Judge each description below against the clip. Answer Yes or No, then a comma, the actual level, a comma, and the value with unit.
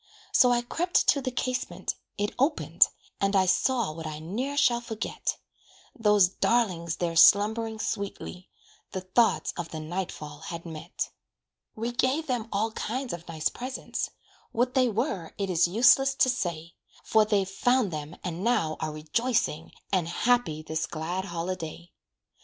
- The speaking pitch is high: Yes, high, 200 Hz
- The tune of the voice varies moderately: No, wide, 6.3 semitones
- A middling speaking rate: Yes, average, 155 wpm